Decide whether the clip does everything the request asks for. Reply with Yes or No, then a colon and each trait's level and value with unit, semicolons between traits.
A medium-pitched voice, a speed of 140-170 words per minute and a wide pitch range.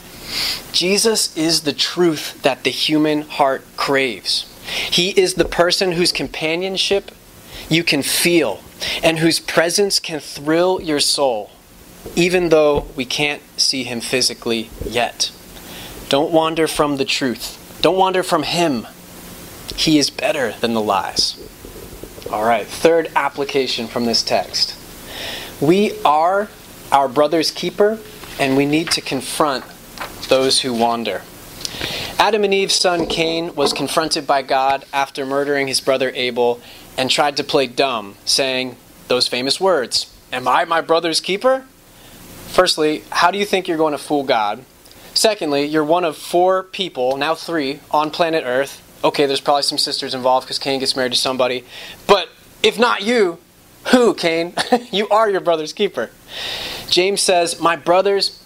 No: medium, 155 Hz; average, 150 wpm; average, 4.6 semitones